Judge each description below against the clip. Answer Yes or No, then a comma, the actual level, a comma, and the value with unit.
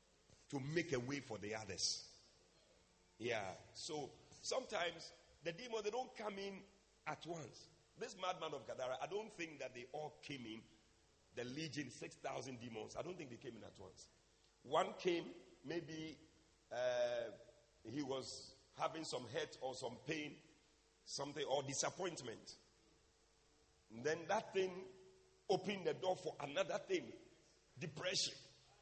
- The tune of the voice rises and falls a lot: Yes, wide, 5.7 semitones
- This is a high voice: No, medium, 155 Hz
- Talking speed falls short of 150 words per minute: Yes, average, 140 wpm